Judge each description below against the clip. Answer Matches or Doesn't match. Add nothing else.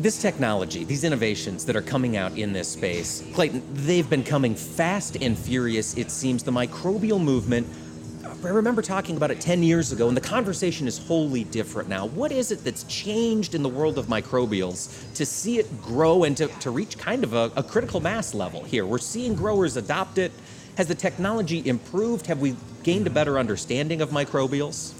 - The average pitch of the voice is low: Doesn't match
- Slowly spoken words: Doesn't match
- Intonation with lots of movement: Matches